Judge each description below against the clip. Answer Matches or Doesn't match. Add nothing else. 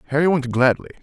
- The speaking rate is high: Doesn't match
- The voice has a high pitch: Doesn't match